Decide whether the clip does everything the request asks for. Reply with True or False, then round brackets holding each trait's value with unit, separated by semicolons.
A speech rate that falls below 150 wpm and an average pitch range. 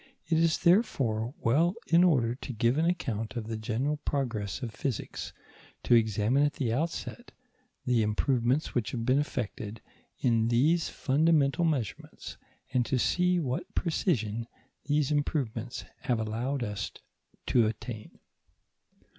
True (135 wpm; 4.8 semitones)